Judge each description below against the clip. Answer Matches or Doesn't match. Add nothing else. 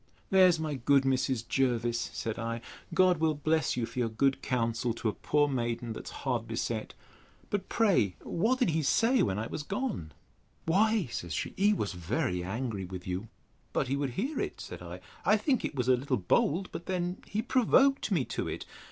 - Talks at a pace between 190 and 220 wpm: Matches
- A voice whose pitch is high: Doesn't match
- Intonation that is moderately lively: Doesn't match